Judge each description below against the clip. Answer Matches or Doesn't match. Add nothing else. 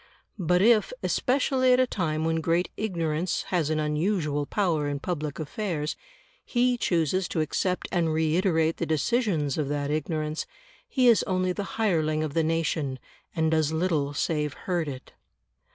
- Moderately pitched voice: Matches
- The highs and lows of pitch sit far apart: Doesn't match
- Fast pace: Doesn't match